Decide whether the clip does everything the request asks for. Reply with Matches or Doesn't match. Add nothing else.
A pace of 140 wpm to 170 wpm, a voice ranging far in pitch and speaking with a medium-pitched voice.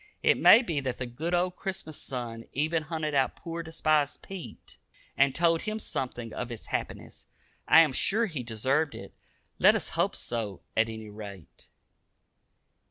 Matches